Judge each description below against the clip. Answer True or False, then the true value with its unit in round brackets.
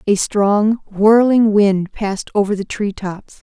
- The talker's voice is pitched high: True (205 Hz)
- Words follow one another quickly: False (155 wpm)